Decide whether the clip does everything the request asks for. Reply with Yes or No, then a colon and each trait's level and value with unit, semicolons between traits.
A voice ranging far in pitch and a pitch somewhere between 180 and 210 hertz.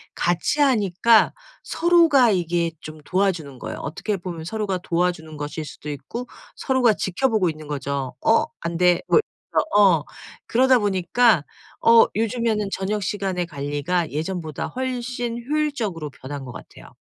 Yes: wide, 6.5 semitones; medium, 185 Hz